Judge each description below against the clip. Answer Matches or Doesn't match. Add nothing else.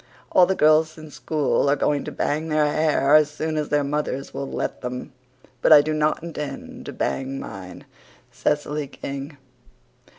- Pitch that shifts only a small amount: Matches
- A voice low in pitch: Doesn't match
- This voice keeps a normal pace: Matches